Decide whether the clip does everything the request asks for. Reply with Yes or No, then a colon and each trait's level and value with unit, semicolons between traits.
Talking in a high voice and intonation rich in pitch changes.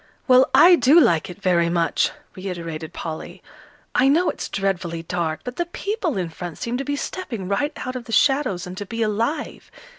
Yes: high, 205 Hz; wide, 7.9 semitones